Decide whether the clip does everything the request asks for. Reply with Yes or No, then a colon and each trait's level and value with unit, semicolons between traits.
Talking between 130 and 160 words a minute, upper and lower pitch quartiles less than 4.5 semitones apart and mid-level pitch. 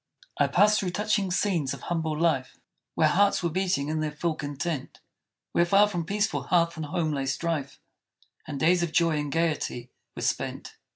No: average, 180 wpm; average, 3.3 semitones; medium, 165 Hz